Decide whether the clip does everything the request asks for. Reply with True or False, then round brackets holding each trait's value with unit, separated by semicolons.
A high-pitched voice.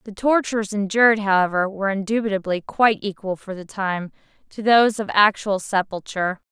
True (200 Hz)